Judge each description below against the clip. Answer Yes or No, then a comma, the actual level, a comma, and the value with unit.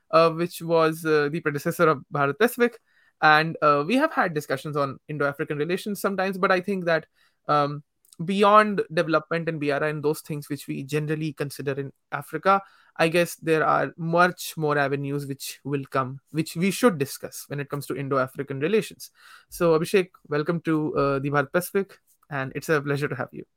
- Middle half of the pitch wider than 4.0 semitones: No, average, 3.5 semitones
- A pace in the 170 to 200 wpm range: Yes, average, 185 wpm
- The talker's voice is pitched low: No, medium, 155 Hz